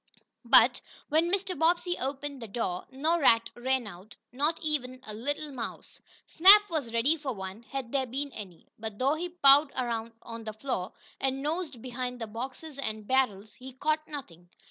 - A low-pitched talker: No, very high, 260 Hz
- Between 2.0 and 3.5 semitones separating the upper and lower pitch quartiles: No, average, 4.8 semitones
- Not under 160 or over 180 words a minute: Yes, average, 175 wpm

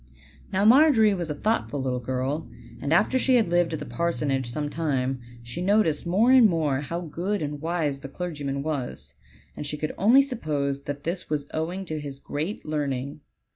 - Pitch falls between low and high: Yes, medium, 155 Hz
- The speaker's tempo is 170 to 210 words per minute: Yes, average, 185 wpm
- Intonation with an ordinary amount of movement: Yes, average, 4.6 semitones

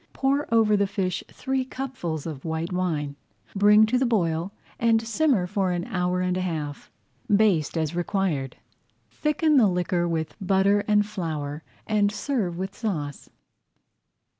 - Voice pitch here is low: No, high, 190 Hz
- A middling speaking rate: Yes, average, 150 wpm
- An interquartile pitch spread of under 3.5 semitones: No, average, 4.6 semitones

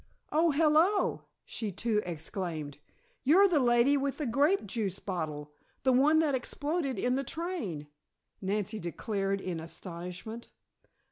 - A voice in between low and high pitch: No, high, 230 Hz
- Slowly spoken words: Yes, slow, 130 wpm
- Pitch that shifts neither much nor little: No, wide, 8.0 semitones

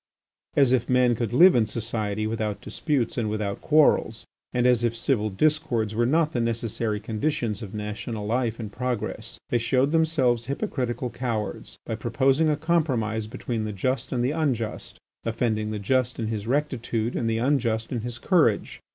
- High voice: No, low, 120 Hz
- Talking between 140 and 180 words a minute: Yes, average, 170 wpm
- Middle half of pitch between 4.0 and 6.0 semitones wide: No, average, 3.1 semitones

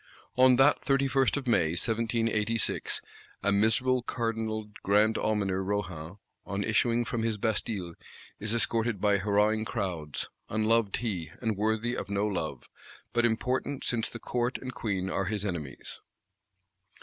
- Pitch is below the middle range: Yes, low, 110 Hz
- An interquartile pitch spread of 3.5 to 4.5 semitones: No, average, 2.8 semitones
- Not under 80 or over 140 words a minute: Yes, slow, 135 wpm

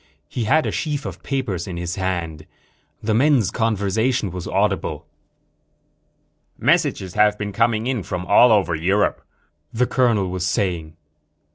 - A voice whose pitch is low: Yes, low, 105 Hz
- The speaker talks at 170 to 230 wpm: No, average, 140 wpm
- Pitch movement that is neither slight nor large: Yes, average, 5.0 semitones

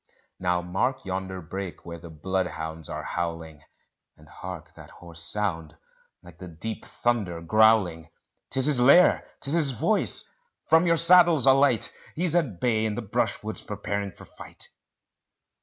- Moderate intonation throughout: No, wide, 7.1 semitones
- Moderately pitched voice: No, very low, 95 Hz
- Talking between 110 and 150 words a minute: Yes, average, 145 wpm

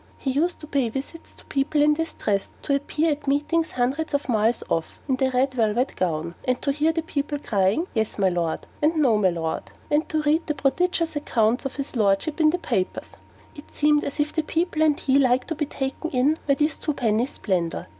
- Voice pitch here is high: Yes, very high, 280 Hz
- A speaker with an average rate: No, fast, 215 wpm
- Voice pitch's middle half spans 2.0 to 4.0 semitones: No, average, 5.0 semitones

